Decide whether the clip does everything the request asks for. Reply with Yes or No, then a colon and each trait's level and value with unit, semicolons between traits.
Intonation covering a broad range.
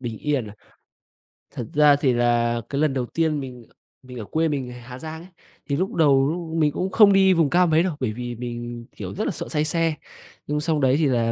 No: average, 4.7 semitones